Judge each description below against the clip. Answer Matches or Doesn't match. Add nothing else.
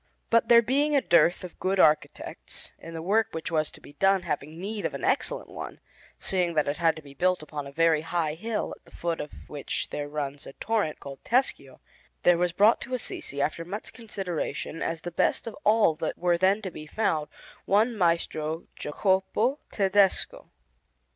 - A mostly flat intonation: Doesn't match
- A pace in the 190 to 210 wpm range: Matches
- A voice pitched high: Doesn't match